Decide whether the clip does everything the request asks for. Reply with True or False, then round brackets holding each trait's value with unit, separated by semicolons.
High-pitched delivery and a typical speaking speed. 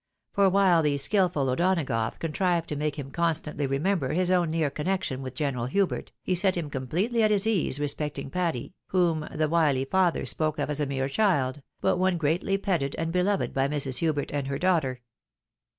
False (155 Hz; 190 wpm)